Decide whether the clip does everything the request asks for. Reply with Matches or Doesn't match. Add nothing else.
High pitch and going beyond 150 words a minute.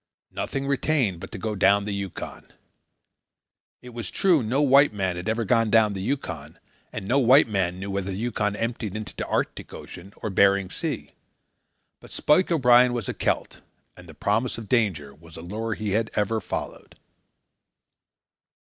Doesn't match